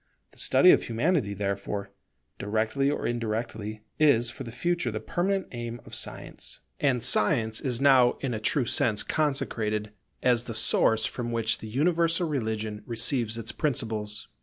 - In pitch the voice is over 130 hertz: No, low, 115 Hz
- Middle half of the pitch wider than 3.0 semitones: Yes, average, 4.0 semitones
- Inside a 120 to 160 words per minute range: Yes, average, 155 wpm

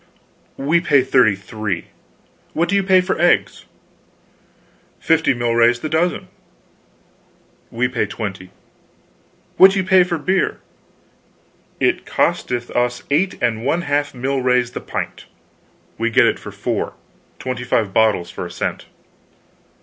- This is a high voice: No, low, 125 Hz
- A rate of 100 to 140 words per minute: Yes, slow, 135 wpm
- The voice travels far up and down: Yes, wide, 6.4 semitones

